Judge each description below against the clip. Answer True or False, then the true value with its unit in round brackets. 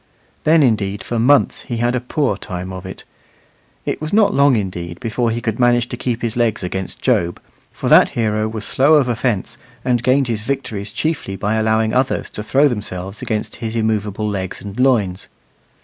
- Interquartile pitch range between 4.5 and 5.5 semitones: False (3.8 semitones)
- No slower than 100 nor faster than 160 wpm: False (190 wpm)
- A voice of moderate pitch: False (110 Hz)